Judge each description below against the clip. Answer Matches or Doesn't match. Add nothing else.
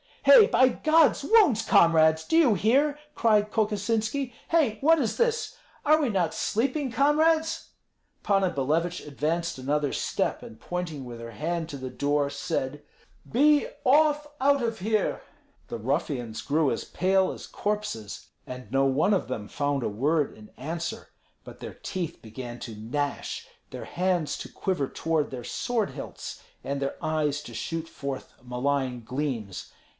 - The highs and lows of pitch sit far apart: Matches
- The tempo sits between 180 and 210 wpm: Doesn't match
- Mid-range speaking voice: Matches